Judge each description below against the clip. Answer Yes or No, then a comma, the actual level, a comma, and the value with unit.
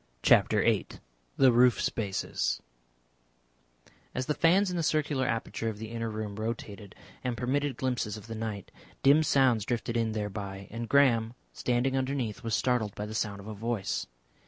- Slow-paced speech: No, average, 165 wpm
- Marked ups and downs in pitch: No, average, 3.4 semitones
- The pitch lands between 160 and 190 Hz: No, low, 115 Hz